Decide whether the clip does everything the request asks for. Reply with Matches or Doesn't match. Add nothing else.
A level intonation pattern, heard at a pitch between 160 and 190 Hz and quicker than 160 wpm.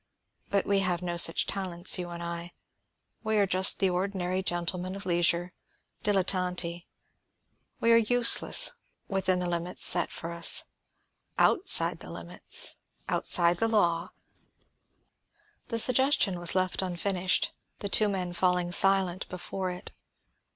Doesn't match